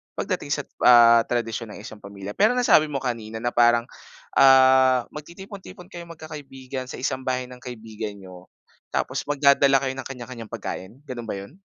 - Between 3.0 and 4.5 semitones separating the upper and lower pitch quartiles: Yes, average, 3.5 semitones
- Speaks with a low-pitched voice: Yes, low, 130 Hz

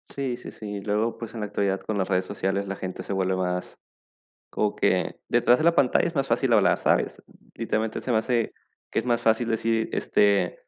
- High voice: No, low, 110 Hz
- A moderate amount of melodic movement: Yes, average, 3.1 semitones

